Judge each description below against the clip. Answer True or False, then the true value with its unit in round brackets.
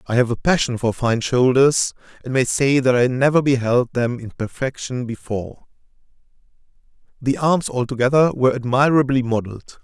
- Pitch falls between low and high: False (130 Hz)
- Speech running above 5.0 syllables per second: True (5.2 syllables/s)